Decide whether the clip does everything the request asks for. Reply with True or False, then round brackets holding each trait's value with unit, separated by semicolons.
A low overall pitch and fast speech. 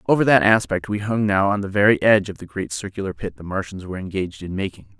True (100 Hz; 250 wpm)